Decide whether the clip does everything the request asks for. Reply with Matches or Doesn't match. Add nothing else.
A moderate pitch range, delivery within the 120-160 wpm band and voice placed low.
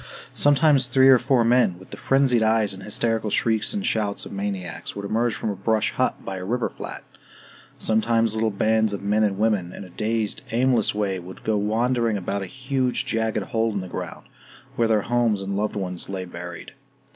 Doesn't match